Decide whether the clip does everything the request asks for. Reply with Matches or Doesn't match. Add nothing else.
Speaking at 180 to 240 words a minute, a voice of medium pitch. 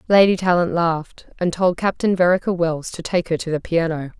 Matches